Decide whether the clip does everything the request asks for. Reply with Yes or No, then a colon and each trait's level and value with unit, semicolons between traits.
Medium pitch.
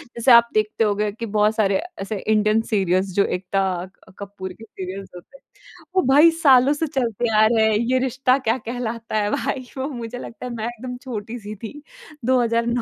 No: high, 225 Hz